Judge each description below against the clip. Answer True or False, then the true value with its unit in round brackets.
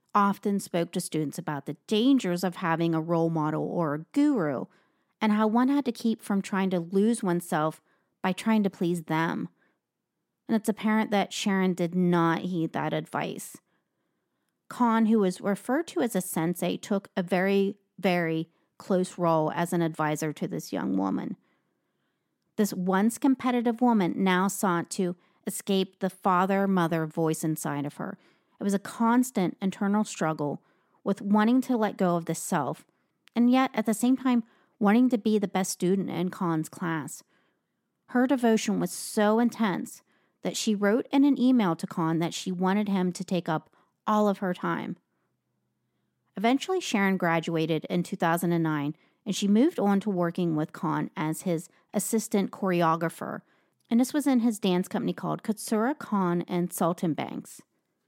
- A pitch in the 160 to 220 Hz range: True (190 Hz)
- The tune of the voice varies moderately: True (4.3 semitones)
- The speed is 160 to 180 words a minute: True (165 wpm)